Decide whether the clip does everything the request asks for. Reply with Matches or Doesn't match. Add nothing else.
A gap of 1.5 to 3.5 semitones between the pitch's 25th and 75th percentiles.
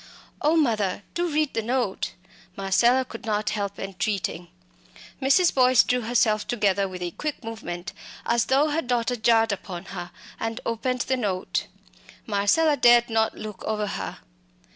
Doesn't match